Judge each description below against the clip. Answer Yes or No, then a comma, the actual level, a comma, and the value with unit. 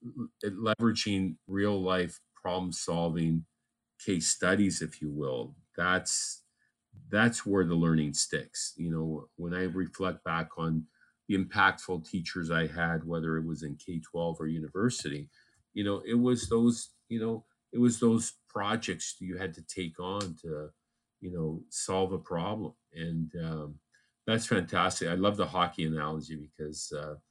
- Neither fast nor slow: Yes, average, 150 wpm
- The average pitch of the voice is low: Yes, very low, 85 Hz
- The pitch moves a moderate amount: Yes, average, 3.8 semitones